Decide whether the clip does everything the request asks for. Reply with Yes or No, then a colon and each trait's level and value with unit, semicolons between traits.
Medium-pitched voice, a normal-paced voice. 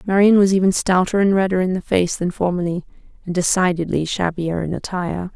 Yes: medium, 180 Hz; average, 180 wpm